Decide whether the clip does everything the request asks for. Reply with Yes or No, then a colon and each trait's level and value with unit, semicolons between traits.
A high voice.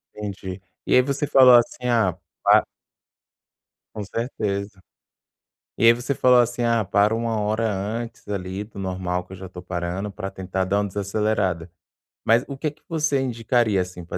No: low, 105 Hz